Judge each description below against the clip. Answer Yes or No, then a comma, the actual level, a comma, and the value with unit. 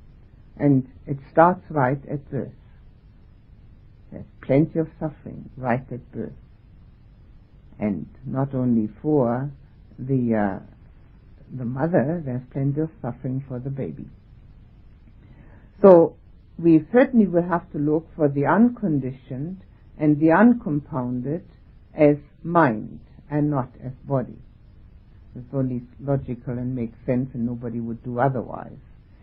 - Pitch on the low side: Yes, low, 130 Hz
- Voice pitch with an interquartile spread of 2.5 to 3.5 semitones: No, average, 4.2 semitones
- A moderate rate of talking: No, slow, 120 wpm